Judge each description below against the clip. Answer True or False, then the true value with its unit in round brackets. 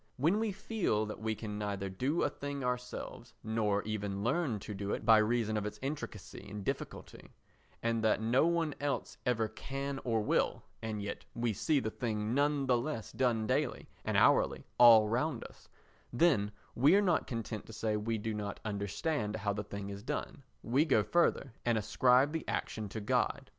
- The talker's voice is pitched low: True (115 Hz)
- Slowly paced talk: False (190 wpm)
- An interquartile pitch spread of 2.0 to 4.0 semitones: False (4.6 semitones)